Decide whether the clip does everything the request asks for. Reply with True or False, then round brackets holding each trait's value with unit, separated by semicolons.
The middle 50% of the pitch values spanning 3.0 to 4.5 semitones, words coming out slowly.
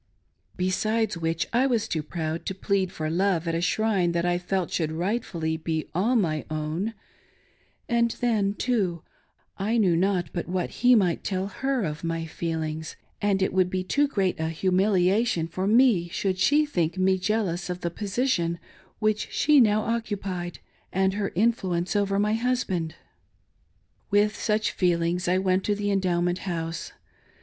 False (3.7 semitones; 165 wpm)